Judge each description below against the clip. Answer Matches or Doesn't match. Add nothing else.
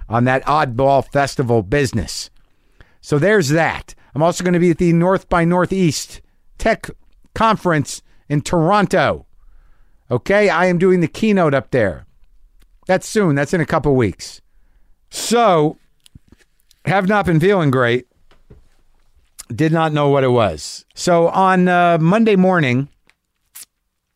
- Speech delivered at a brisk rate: Doesn't match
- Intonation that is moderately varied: Doesn't match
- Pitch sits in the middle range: Matches